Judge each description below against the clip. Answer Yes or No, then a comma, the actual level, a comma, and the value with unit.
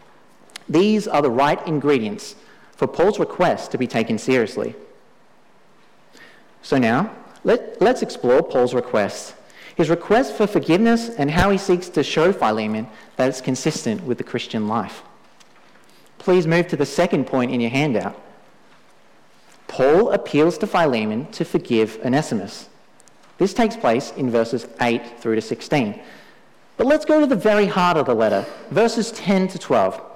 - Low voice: No, medium, 170 Hz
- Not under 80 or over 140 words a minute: No, average, 150 wpm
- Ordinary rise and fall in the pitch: No, wide, 8.6 semitones